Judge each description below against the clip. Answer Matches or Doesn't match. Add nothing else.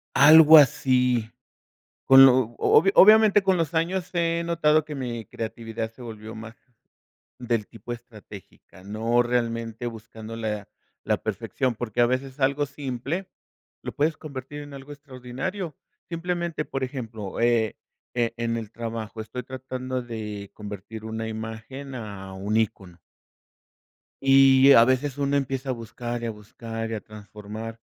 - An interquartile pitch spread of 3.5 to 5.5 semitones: Matches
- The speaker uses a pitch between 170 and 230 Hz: Doesn't match